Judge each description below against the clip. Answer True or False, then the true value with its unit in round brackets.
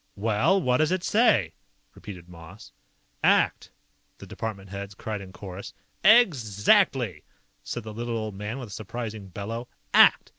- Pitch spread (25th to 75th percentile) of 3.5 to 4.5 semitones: True (4.1 semitones)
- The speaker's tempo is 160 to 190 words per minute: False (145 wpm)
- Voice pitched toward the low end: True (110 Hz)